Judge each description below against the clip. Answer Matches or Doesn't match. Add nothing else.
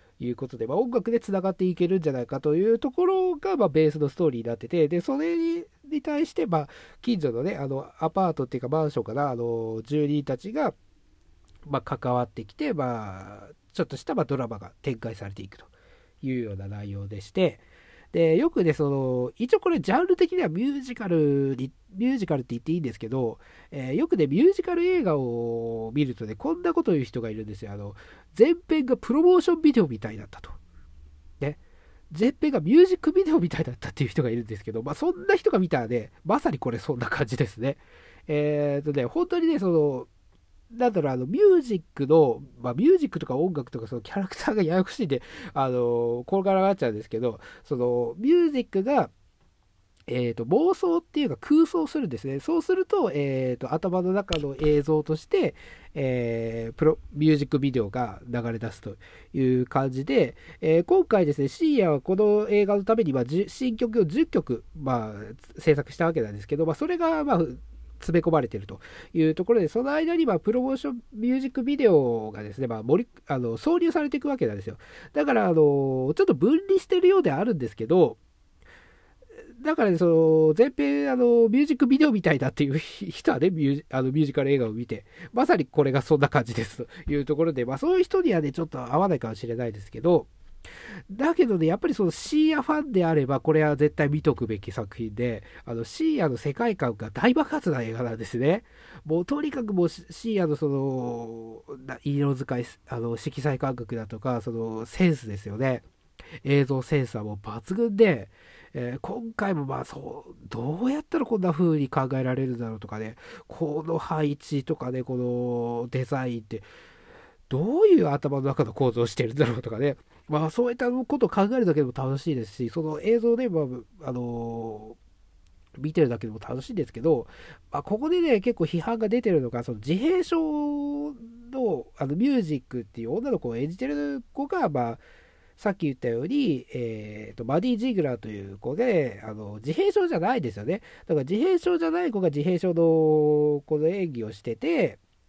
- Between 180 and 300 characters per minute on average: Doesn't match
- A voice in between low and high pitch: Matches